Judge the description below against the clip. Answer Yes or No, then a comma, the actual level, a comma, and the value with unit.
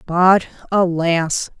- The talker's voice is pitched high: No, medium, 175 Hz